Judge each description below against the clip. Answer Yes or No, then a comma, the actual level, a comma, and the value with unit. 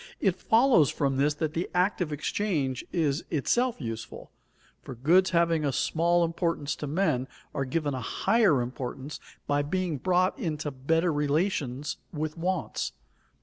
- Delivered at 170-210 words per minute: No, average, 150 wpm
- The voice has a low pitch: No, medium, 155 Hz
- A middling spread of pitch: Yes, average, 4.0 semitones